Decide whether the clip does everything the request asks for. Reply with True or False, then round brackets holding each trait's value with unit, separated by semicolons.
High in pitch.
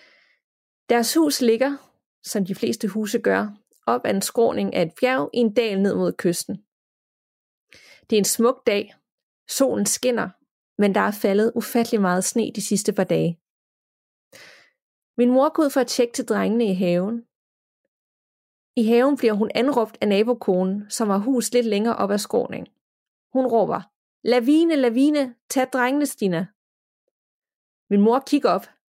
True (230 Hz)